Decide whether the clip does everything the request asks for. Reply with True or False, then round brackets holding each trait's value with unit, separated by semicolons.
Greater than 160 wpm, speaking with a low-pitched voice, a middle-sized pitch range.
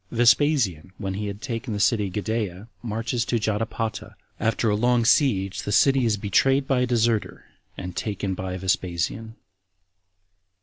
False (145 wpm; 110 Hz; 3.4 semitones)